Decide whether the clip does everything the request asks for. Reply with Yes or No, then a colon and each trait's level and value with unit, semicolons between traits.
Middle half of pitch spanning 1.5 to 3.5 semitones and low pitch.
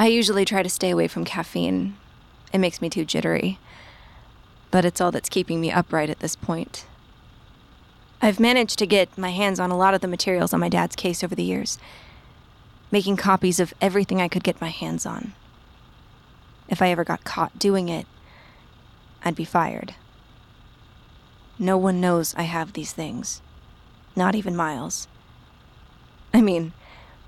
No: average, 2.7 semitones; medium, 180 Hz